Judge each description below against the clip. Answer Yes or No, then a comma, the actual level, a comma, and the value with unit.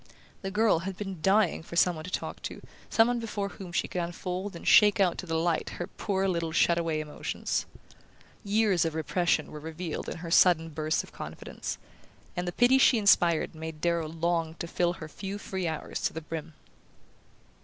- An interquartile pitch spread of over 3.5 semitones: No, average, 3.1 semitones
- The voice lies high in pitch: No, medium, 175 Hz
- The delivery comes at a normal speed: Yes, average, 195 wpm